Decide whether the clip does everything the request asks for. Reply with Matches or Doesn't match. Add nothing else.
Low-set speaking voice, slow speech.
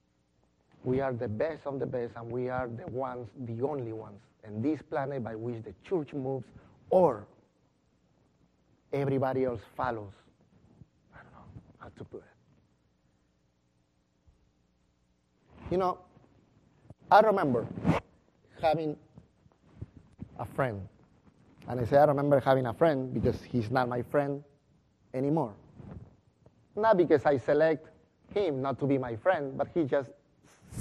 Matches